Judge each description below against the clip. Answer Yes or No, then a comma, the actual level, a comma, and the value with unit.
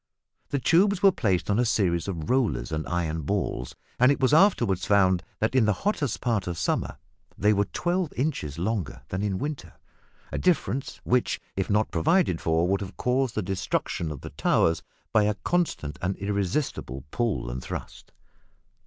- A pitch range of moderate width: No, wide, 6.9 semitones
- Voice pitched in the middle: No, low, 100 Hz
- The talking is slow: No, average, 175 wpm